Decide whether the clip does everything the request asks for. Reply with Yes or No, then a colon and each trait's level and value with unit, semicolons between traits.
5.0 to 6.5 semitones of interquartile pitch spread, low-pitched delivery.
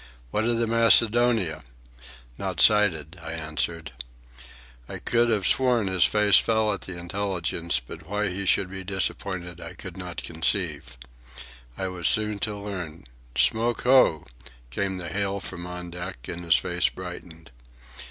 No: average, 3.6 semitones; very low, 95 Hz